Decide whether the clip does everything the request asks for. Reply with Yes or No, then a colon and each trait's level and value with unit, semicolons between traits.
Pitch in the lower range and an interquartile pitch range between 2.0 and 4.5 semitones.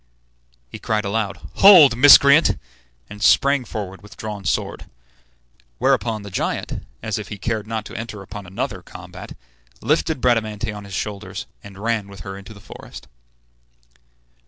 Yes: low, 105 Hz; narrow, 2.5 semitones